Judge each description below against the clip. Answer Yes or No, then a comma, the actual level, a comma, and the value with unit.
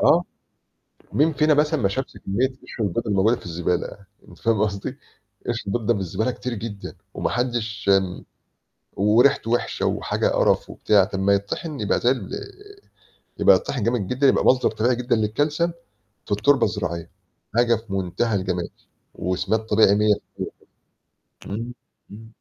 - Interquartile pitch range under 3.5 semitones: No, average, 4.1 semitones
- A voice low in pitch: Yes, low, 110 Hz